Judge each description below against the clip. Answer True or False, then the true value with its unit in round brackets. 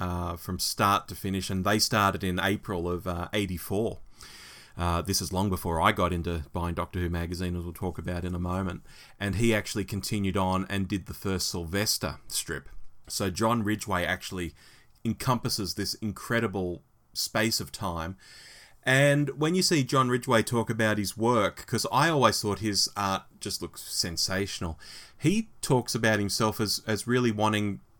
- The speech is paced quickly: False (170 wpm)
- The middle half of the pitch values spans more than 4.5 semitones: False (3.4 semitones)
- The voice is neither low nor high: False (100 Hz)